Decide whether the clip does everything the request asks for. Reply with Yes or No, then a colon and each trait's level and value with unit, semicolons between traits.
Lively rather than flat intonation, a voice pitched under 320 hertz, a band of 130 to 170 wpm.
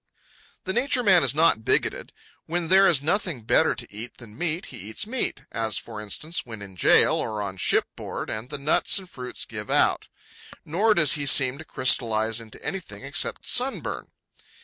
No: wide, 8.0 semitones; medium, 140 Hz; average, 180 wpm